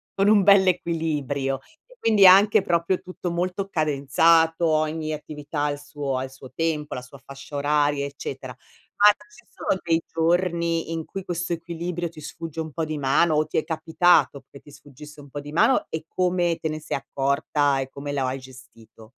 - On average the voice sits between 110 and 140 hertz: No, medium, 155 Hz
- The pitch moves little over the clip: No, average, 3.3 semitones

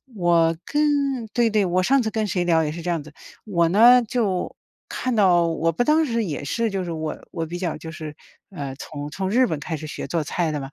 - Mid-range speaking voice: Yes, medium, 175 Hz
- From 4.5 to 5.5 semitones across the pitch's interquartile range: Yes, average, 5.1 semitones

